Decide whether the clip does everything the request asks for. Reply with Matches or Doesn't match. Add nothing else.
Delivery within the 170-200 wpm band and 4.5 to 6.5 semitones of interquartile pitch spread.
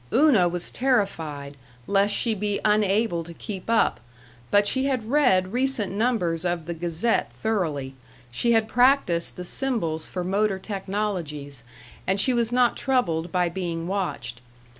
Doesn't match